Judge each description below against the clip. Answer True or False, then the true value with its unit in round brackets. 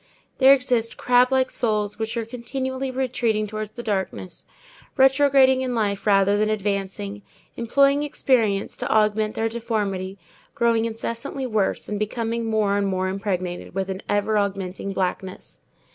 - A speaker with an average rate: True (145 wpm)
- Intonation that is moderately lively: True (3.6 semitones)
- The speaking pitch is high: True (220 Hz)